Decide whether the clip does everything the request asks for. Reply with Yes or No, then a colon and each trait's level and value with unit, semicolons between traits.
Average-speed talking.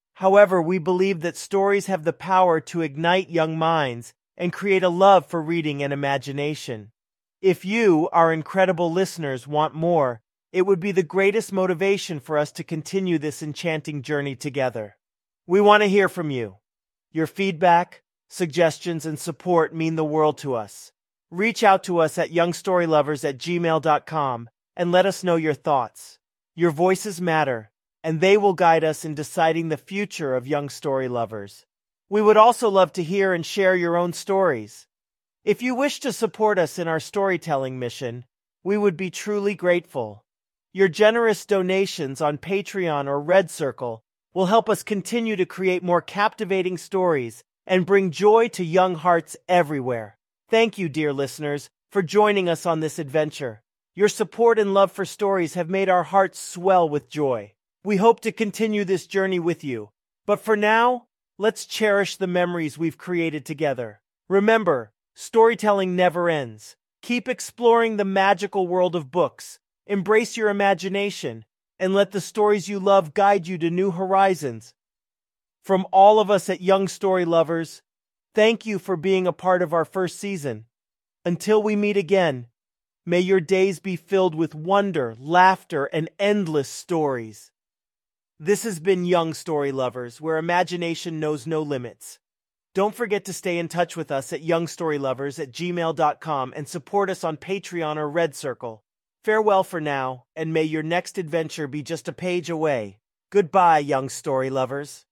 Yes: average, 160 wpm